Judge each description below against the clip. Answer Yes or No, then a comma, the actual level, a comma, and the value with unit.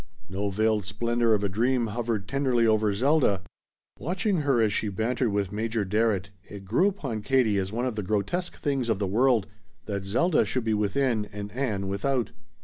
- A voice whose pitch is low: Yes, low, 110 Hz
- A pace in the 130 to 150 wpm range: No, average, 185 wpm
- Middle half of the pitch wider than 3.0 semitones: Yes, average, 3.9 semitones